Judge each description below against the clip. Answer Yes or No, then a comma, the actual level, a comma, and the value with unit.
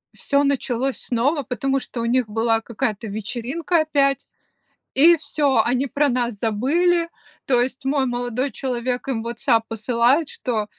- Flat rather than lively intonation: No, average, 3.1 semitones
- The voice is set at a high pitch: Yes, very high, 250 Hz